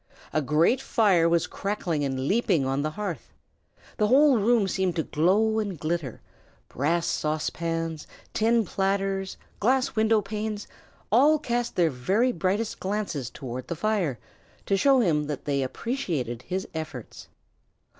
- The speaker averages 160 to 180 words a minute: No, average, 140 wpm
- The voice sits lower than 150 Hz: No, medium, 185 Hz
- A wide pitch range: Yes, wide, 6.0 semitones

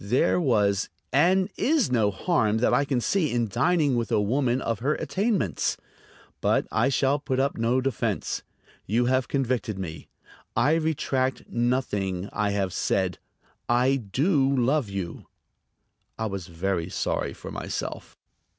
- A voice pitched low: Yes, low, 125 Hz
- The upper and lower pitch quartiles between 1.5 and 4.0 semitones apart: No, average, 5.1 semitones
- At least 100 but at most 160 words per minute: Yes, average, 145 wpm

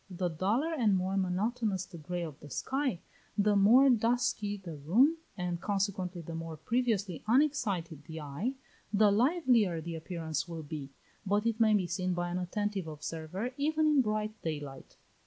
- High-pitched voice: Yes, high, 195 Hz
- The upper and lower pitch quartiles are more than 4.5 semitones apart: Yes, average, 5.1 semitones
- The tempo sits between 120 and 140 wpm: No, average, 165 wpm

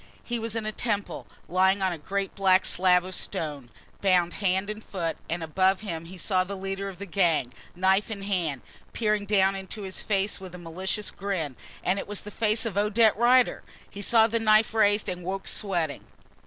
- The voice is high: Yes, high, 195 Hz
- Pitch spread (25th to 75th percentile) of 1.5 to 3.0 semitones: Yes, narrow, 2.5 semitones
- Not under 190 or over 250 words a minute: Yes, average, 200 wpm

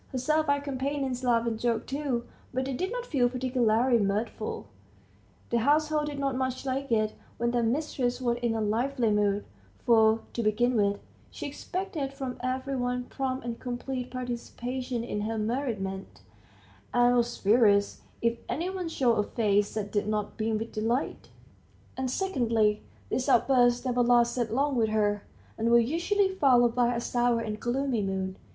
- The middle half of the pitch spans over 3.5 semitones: No, average, 2.9 semitones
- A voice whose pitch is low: No, high, 245 Hz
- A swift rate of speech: No, average, 165 wpm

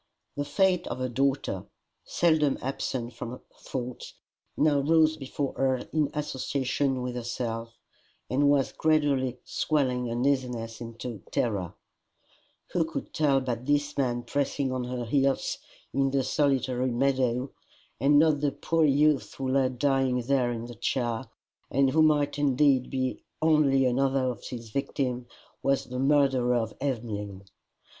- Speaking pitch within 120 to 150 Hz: Yes, low, 135 Hz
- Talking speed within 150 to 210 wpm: No, average, 140 wpm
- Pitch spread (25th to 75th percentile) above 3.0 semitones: No, narrow, 2.6 semitones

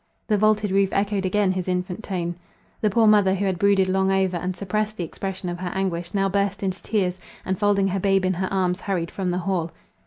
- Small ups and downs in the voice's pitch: Yes, narrow, 1.6 semitones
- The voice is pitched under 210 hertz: Yes, high, 190 Hz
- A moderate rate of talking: No, fast, 225 wpm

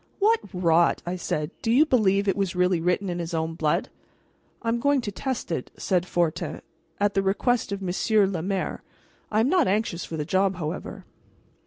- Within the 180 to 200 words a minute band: Yes, average, 195 wpm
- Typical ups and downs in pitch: Yes, average, 4.0 semitones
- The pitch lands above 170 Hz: Yes, high, 190 Hz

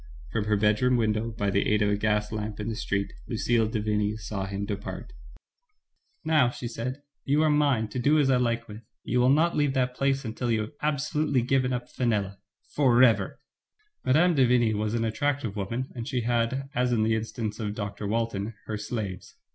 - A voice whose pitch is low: Yes, low, 115 Hz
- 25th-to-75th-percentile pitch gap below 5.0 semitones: Yes, average, 3.3 semitones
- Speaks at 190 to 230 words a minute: Yes, fast, 205 wpm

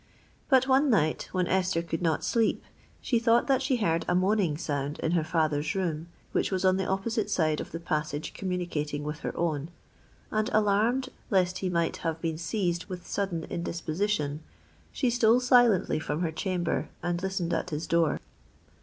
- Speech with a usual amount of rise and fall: Yes, average, 4.4 semitones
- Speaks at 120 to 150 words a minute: No, average, 175 wpm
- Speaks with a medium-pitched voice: Yes, medium, 180 Hz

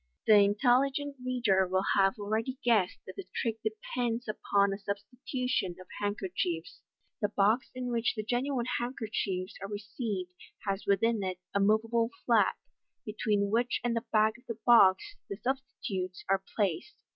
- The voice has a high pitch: Yes, high, 215 Hz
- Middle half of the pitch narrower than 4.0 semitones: Yes, average, 3.5 semitones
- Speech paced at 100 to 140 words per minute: No, average, 150 wpm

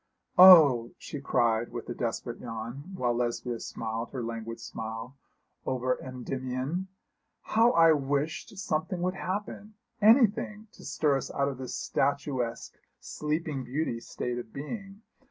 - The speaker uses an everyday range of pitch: No, wide, 5.7 semitones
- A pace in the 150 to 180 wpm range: No, slow, 135 wpm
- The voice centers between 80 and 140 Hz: Yes, low, 135 Hz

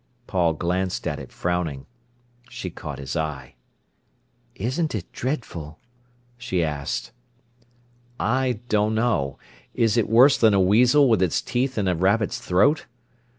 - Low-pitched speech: Yes, low, 105 Hz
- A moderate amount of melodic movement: No, wide, 5.8 semitones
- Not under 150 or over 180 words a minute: No, slow, 135 wpm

